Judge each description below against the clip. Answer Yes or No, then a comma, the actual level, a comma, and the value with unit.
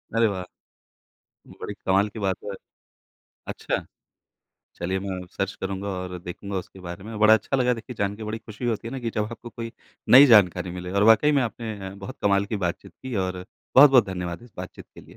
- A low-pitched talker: Yes, low, 100 Hz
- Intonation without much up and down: No, average, 3.5 semitones